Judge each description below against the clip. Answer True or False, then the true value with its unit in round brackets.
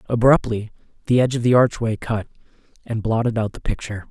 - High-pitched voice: False (115 Hz)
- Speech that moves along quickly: False (175 wpm)